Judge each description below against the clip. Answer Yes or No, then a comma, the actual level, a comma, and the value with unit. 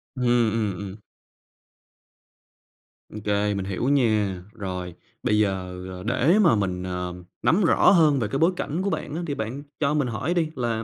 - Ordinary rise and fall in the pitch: No, wide, 6.8 semitones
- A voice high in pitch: No, low, 110 Hz